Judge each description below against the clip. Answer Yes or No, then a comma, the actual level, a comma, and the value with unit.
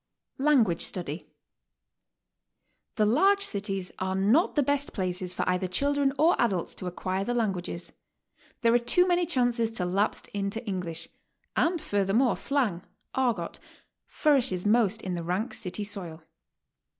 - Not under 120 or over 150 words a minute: Yes, average, 140 wpm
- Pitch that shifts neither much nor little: No, wide, 5.9 semitones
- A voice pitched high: Yes, high, 210 Hz